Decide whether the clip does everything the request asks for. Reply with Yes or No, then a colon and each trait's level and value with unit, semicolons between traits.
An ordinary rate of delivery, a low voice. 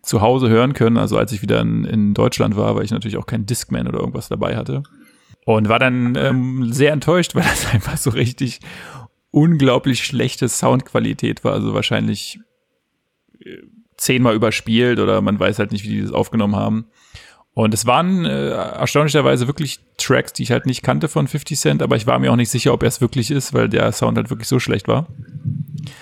No: fast, 195 wpm; low, 125 Hz